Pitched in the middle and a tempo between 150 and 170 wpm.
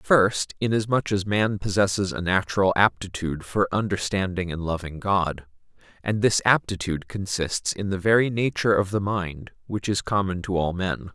No: very low, 95 Hz; average, 160 wpm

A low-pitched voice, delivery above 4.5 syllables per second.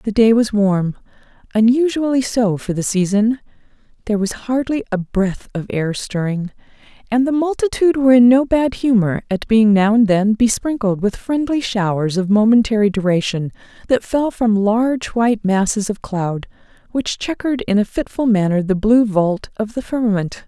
No: high, 220 Hz; 5.0 syllables/s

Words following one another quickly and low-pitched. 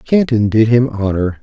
No: average, 170 wpm; low, 115 Hz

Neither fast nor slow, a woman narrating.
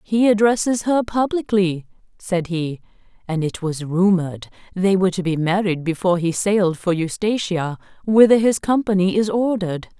Yes: average, 150 wpm; female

